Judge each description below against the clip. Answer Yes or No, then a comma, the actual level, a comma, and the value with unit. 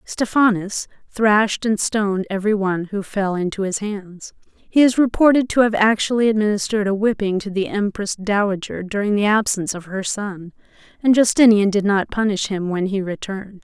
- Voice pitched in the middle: No, high, 205 Hz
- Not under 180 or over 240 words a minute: No, average, 170 wpm